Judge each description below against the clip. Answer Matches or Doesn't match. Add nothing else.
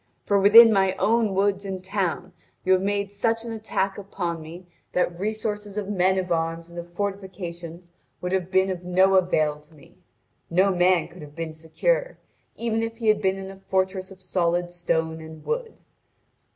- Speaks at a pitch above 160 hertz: Matches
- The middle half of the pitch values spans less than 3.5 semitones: Matches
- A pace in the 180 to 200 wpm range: Matches